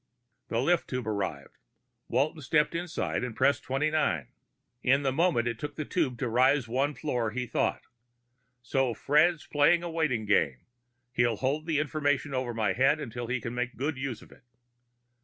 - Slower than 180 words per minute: No, average, 185 wpm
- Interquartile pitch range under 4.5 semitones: Yes, average, 4.0 semitones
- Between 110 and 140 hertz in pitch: Yes, low, 135 Hz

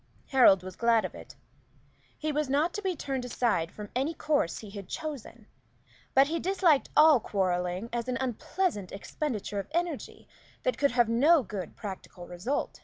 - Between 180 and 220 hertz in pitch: No, very high, 250 Hz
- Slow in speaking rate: No, average, 170 wpm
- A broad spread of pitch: Yes, wide, 7.1 semitones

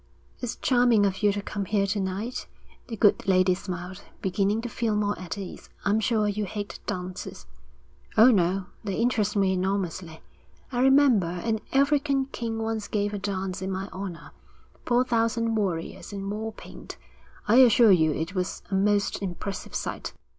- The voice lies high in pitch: Yes, high, 205 Hz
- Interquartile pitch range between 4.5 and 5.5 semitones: No, average, 3.1 semitones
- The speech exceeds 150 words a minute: Yes, average, 170 wpm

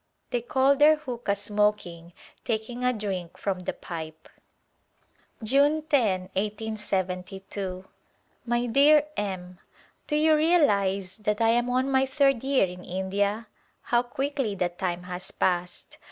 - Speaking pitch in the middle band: No, high, 210 Hz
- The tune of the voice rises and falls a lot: Yes, wide, 6.0 semitones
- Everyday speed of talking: No, slow, 130 wpm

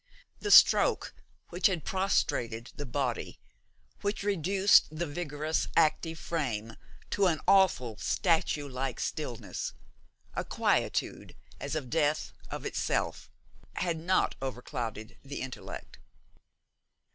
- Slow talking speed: Yes, slow, 110 wpm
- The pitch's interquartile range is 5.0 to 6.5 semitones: Yes, wide, 5.5 semitones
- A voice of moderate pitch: Yes, medium, 155 Hz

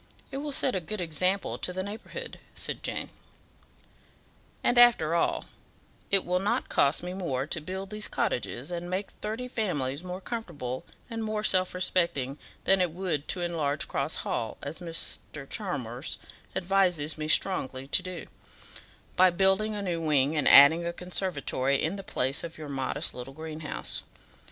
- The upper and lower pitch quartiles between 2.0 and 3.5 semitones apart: No, average, 4.8 semitones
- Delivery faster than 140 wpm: Yes, average, 160 wpm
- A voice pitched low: No, medium, 175 Hz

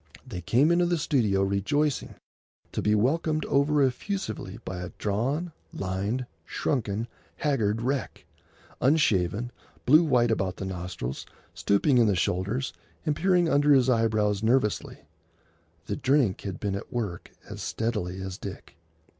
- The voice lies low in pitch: Yes, low, 115 Hz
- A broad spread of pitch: Yes, wide, 6.5 semitones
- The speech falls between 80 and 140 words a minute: Yes, slow, 135 wpm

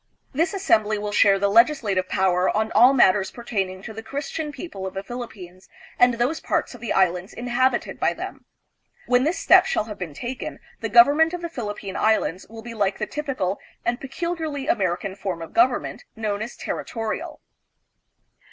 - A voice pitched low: No, high, 225 Hz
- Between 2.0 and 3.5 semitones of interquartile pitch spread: No, average, 5.2 semitones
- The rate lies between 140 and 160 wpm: No, average, 175 wpm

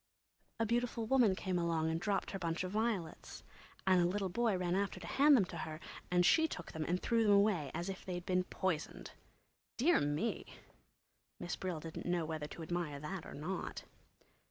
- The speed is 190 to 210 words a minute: Yes, average, 195 wpm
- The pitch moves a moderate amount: Yes, average, 3.7 semitones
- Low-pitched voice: No, medium, 180 Hz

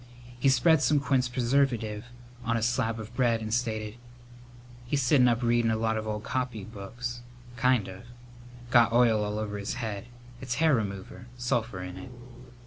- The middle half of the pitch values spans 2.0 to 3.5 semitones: Yes, narrow, 2.5 semitones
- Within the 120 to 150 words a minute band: No, average, 165 wpm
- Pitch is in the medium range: No, low, 115 Hz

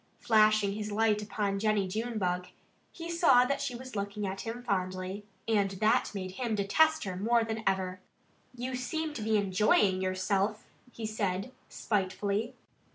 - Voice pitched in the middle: No, high, 210 Hz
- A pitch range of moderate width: Yes, average, 3.0 semitones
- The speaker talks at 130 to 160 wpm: Yes, average, 155 wpm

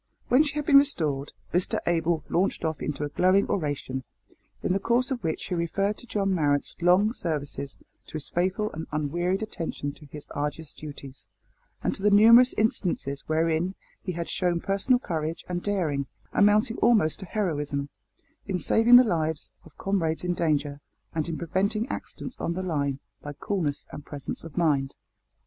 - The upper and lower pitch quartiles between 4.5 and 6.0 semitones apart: Yes, average, 5.1 semitones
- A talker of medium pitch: Yes, medium, 170 Hz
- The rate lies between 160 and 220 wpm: Yes, average, 170 wpm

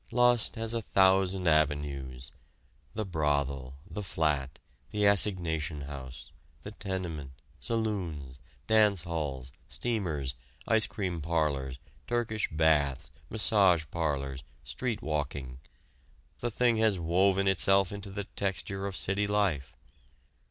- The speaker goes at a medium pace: No, slow, 110 wpm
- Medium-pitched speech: No, very low, 85 Hz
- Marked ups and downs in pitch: Yes, wide, 5.9 semitones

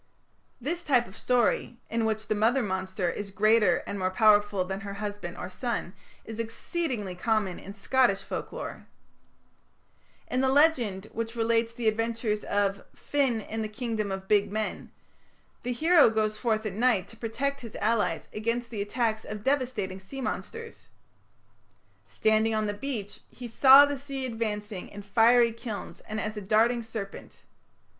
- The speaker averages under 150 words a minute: No, average, 160 wpm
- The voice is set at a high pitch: Yes, high, 220 Hz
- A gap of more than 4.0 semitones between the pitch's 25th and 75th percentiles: No, average, 2.8 semitones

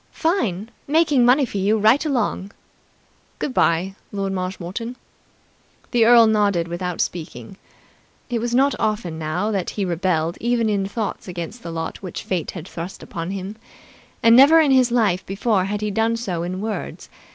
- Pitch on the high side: Yes, high, 205 Hz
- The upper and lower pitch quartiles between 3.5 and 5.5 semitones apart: Yes, average, 4.6 semitones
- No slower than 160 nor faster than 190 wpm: Yes, average, 165 wpm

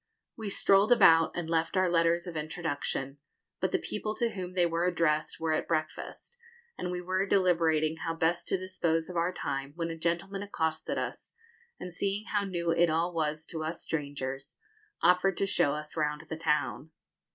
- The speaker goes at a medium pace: Yes, average, 185 wpm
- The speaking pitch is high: No, medium, 165 Hz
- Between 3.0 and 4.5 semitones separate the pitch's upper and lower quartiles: No, narrow, 2.5 semitones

